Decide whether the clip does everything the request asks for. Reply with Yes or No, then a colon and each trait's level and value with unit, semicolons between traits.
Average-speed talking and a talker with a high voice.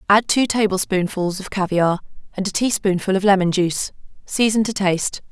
Yes: average, 160 wpm; high, 195 Hz